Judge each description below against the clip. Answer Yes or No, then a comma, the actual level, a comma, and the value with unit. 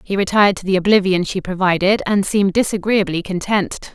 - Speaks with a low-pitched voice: No, high, 195 Hz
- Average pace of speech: Yes, average, 165 wpm